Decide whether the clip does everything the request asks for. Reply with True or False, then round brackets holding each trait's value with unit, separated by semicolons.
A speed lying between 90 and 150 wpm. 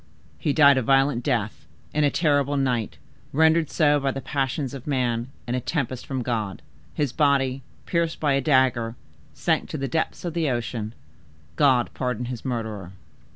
False (170 wpm)